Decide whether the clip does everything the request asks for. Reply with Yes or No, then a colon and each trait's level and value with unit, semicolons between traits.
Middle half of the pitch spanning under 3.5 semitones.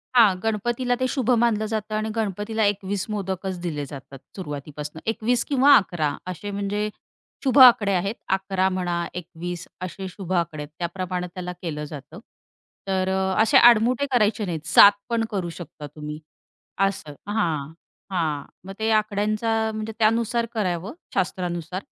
No: average, 4.0 semitones